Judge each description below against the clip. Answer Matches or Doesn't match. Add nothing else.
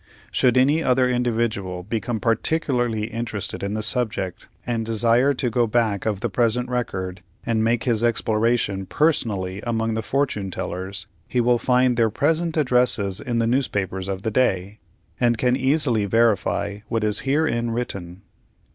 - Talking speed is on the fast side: Doesn't match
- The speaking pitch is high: Doesn't match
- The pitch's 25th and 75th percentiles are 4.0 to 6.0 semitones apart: Doesn't match